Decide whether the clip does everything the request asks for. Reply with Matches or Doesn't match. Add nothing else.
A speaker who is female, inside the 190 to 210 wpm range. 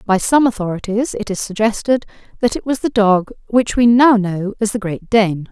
Matches